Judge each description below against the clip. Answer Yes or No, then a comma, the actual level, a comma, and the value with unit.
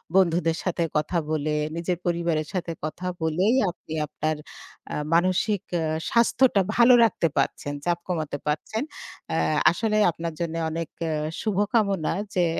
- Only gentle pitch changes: No, average, 3.7 semitones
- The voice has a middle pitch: Yes, medium, 170 Hz